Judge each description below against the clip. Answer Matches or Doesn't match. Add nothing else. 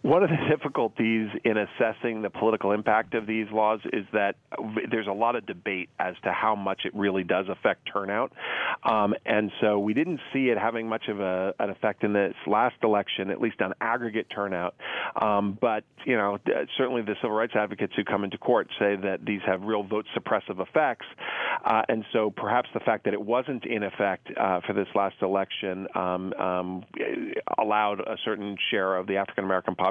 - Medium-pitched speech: Doesn't match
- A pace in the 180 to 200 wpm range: Matches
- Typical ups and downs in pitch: Doesn't match